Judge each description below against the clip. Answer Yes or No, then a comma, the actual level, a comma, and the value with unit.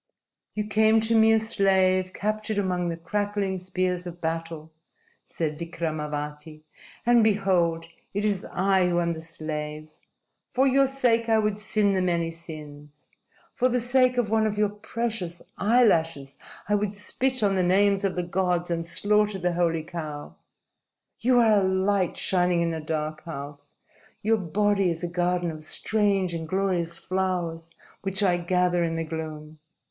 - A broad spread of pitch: No, average, 4.0 semitones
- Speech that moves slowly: No, average, 160 wpm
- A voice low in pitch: No, medium, 185 Hz